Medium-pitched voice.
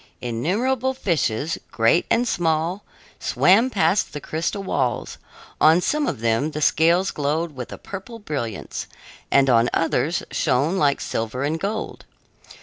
Yes: medium, 160 Hz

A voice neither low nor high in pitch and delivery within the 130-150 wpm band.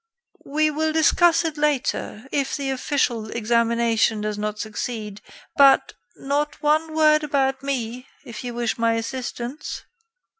No: very high, 265 Hz; slow, 135 wpm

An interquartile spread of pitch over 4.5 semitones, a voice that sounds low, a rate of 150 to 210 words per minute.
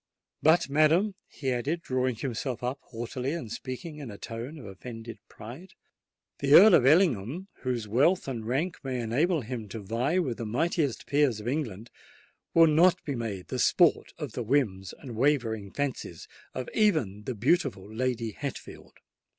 Yes: average, 4.9 semitones; low, 130 Hz; average, 165 wpm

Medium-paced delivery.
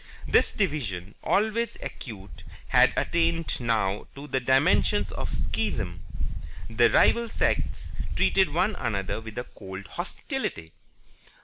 No: slow, 120 wpm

